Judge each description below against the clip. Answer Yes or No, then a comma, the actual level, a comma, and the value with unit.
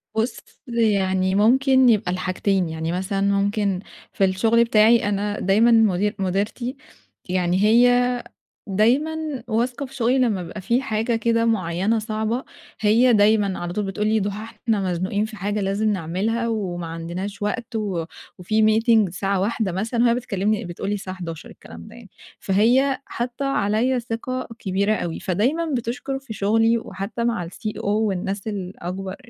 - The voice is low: No, high, 210 Hz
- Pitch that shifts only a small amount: No, average, 3.4 semitones